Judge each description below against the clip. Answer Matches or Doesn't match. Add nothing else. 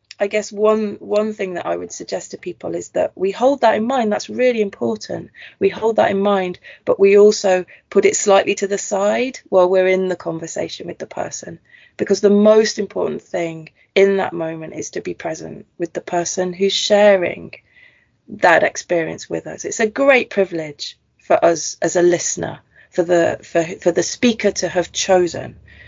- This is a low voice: Doesn't match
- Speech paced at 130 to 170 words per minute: Doesn't match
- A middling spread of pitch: Matches